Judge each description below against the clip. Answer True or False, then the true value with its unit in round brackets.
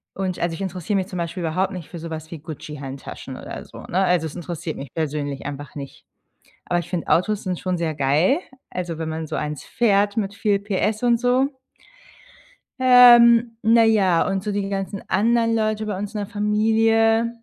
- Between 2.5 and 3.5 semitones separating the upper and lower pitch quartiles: False (5.0 semitones)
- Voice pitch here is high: True (195 Hz)